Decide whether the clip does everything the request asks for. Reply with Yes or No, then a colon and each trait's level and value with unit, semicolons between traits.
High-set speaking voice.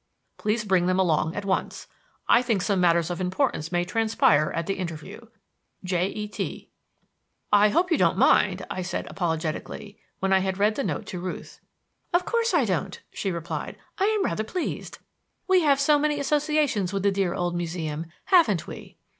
Yes: high, 195 Hz